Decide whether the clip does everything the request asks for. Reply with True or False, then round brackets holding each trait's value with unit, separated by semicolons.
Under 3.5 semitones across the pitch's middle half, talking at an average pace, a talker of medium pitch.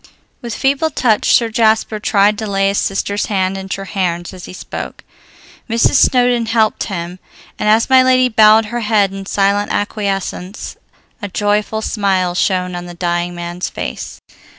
False (2.9 semitones; 160 wpm; 205 Hz)